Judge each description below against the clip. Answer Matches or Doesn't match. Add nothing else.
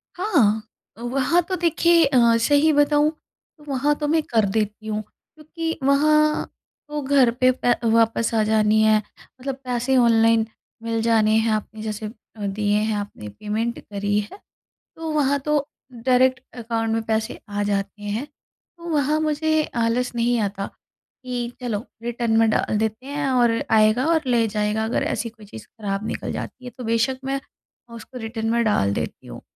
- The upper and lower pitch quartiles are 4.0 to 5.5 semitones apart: Matches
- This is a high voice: Matches